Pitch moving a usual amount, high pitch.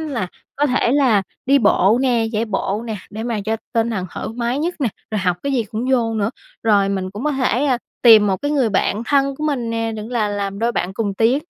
Yes: average, 3.8 semitones; high, 225 Hz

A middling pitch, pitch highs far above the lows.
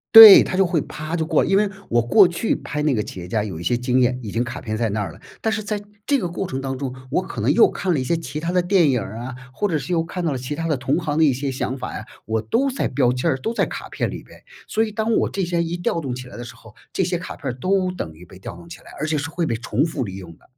Yes: medium, 145 Hz; wide, 6.6 semitones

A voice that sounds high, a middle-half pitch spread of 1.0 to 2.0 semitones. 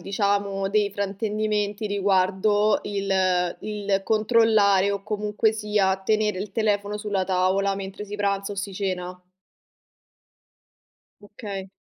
Yes: high, 200 Hz; narrow, 1.3 semitones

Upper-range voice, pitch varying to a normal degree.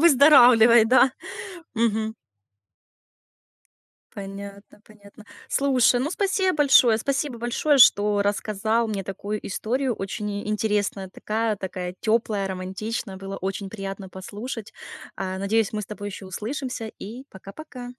Yes: high, 215 Hz; average, 3.5 semitones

